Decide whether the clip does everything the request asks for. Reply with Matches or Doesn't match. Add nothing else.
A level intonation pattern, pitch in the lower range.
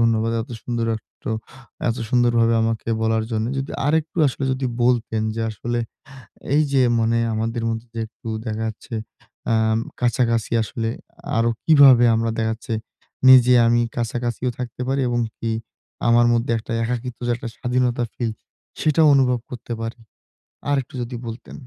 Matches